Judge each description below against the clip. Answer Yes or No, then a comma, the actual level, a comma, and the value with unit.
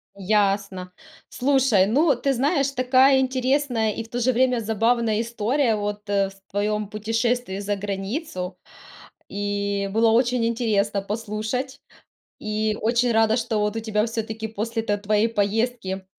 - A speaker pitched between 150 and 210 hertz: No, high, 220 Hz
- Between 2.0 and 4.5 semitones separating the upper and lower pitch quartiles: Yes, average, 3.2 semitones